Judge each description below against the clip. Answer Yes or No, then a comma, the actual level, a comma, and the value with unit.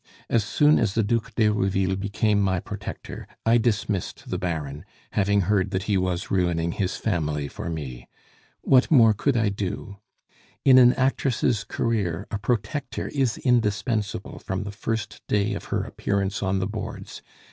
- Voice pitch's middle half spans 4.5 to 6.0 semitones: No, average, 3.3 semitones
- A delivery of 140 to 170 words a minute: Yes, average, 160 wpm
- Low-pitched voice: Yes, low, 100 Hz